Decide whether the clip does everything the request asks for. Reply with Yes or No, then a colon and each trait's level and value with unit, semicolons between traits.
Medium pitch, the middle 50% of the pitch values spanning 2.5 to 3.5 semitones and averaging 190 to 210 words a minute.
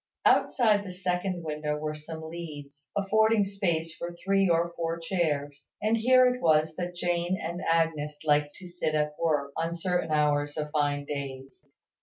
No: medium, 165 Hz; average, 3.1 semitones; average, 165 wpm